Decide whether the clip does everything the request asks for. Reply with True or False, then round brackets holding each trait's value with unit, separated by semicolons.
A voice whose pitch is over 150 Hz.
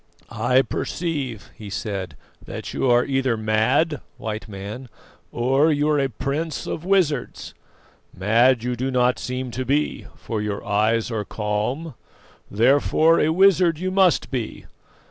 False (130 Hz)